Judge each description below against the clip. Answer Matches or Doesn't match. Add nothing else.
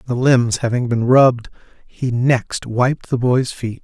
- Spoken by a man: Matches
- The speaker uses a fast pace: Doesn't match